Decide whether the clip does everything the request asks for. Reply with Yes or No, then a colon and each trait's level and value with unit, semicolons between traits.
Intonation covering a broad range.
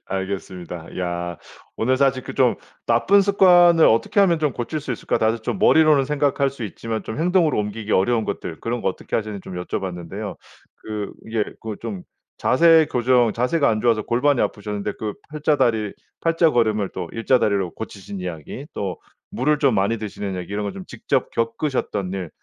Yes: wide, 5.8 semitones